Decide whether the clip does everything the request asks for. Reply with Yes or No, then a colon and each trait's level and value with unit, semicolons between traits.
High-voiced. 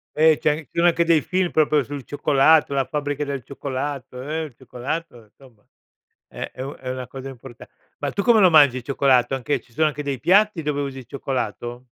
No: medium, 140 Hz